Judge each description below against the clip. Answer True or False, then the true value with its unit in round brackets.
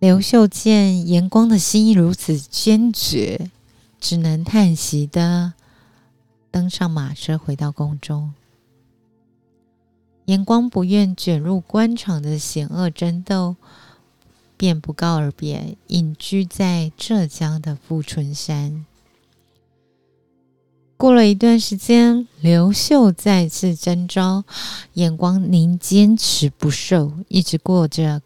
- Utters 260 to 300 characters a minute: False (160 characters per minute)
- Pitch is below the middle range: False (170 Hz)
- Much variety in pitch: False (4.4 semitones)